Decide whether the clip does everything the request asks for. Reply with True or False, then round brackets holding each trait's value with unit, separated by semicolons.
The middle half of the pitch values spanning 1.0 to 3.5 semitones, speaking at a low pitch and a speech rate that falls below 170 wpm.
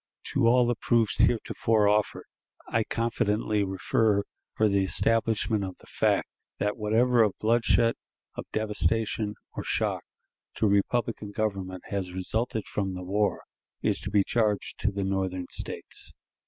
True (2.4 semitones; 105 Hz; 140 wpm)